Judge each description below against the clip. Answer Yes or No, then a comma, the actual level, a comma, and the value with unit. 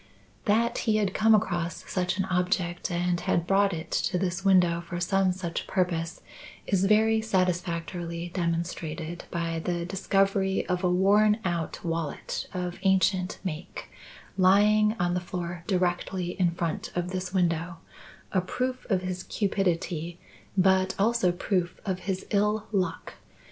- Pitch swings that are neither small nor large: No, narrow, 2.1 semitones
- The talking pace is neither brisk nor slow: Yes, average, 145 wpm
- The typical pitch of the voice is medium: Yes, medium, 180 Hz